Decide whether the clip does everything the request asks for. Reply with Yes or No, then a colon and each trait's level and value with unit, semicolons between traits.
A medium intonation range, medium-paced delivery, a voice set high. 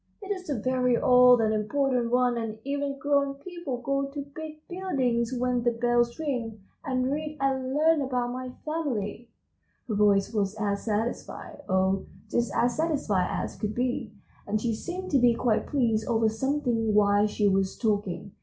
Yes: average, 4.3 semitones; average, 170 wpm; high, 245 Hz